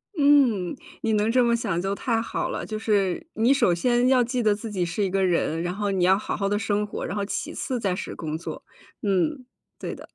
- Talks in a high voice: Yes, high, 210 Hz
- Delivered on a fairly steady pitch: No, average, 3.8 semitones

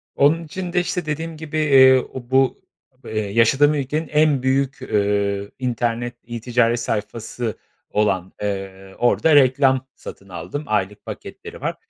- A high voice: No, low, 125 Hz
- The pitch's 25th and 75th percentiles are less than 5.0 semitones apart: No, wide, 5.4 semitones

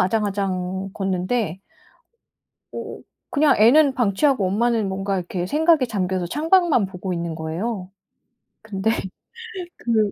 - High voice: Yes, high, 200 Hz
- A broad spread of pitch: No, average, 4.4 semitones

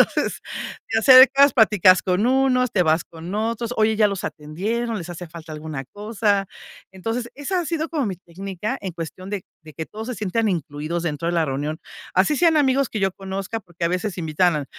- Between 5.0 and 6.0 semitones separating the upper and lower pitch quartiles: Yes, wide, 5.5 semitones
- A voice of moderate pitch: No, high, 195 Hz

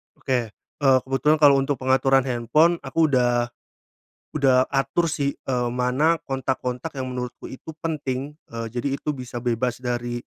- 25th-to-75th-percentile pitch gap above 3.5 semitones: No, narrow, 2.5 semitones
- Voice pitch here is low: Yes, low, 130 Hz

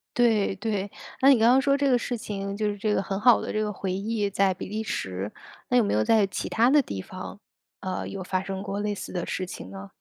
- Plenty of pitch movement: No, average, 3.0 semitones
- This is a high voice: Yes, high, 205 Hz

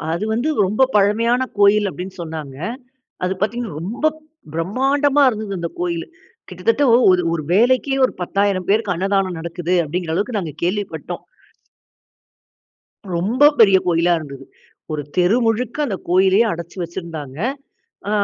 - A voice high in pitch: Yes, high, 195 Hz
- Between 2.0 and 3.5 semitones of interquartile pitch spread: No, average, 4.6 semitones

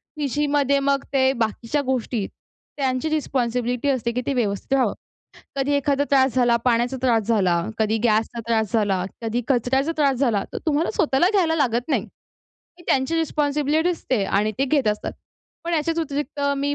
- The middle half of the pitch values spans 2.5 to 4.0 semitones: Yes, average, 3.7 semitones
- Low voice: No, very high, 265 Hz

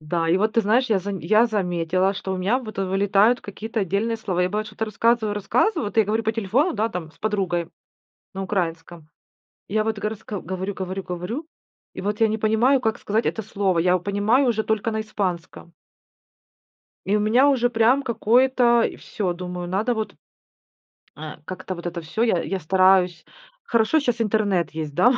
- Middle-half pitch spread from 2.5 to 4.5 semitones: Yes, average, 3.4 semitones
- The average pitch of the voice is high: Yes, high, 205 Hz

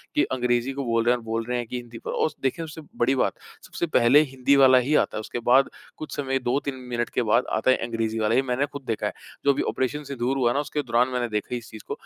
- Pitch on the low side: Yes, low, 125 Hz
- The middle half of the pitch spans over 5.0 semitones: No, narrow, 2.4 semitones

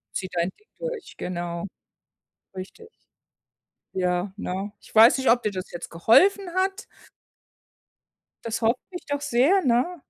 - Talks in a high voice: Yes, high, 230 Hz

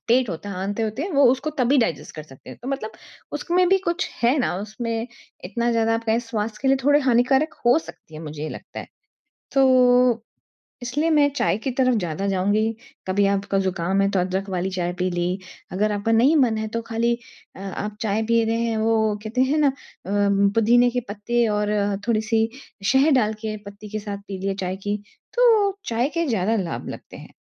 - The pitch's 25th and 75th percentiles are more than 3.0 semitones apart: Yes, average, 4.1 semitones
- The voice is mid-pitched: No, high, 225 Hz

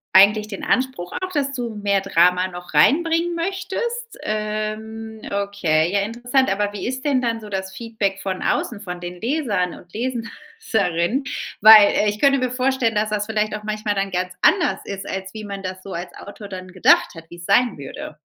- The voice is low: No, high, 210 Hz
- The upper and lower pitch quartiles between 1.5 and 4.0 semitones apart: No, average, 4.6 semitones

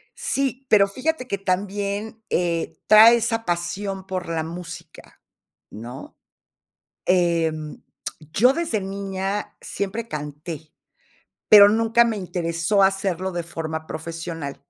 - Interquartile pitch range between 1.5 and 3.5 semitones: No, average, 4.2 semitones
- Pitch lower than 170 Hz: No, high, 190 Hz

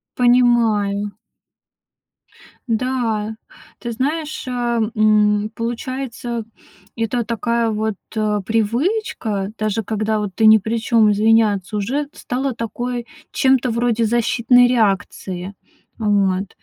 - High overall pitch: Yes, high, 225 Hz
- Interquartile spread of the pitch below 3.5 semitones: Yes, narrow, 2.5 semitones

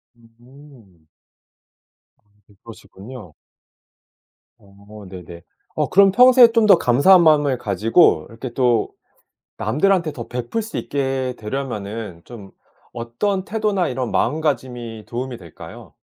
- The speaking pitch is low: Yes, low, 125 Hz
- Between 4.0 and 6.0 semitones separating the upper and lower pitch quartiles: No, wide, 6.4 semitones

